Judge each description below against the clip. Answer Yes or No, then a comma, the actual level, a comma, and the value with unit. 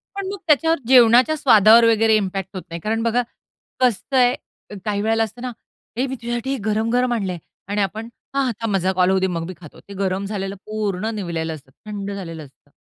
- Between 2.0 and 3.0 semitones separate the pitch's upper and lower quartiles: No, average, 3.9 semitones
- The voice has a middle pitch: No, high, 215 Hz